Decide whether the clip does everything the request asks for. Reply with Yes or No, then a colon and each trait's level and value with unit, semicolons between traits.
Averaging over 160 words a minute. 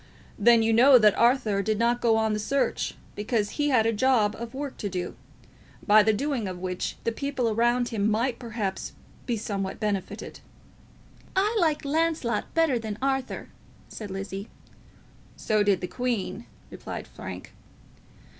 No: average, 155 wpm